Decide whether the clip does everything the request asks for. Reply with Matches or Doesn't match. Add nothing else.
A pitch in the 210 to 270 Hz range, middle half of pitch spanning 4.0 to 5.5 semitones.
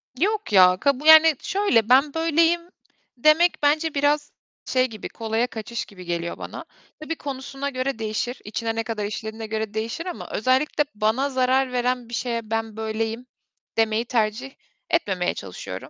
Matches